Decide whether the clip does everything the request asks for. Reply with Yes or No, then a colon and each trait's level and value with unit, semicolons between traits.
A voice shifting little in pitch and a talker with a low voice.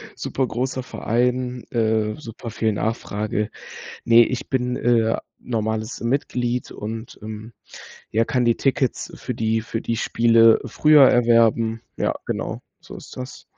Yes: narrow, 1.9 semitones; low, 115 Hz